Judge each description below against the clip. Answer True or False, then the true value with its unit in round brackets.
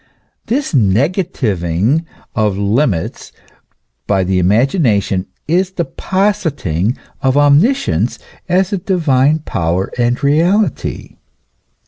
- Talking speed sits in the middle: False (90 wpm)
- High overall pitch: False (135 Hz)